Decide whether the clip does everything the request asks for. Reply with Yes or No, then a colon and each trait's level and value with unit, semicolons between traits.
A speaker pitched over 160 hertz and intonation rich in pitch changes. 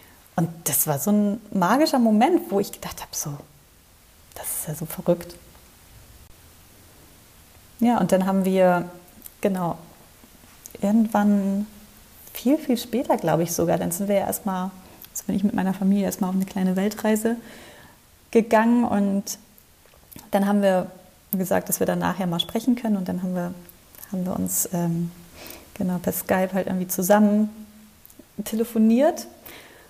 No: high, 190 Hz; average, 3.8 semitones